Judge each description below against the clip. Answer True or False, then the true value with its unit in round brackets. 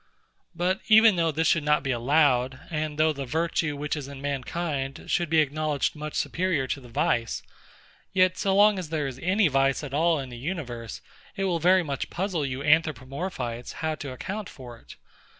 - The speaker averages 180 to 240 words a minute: True (190 wpm)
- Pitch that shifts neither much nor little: True (4.0 semitones)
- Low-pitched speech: False (150 Hz)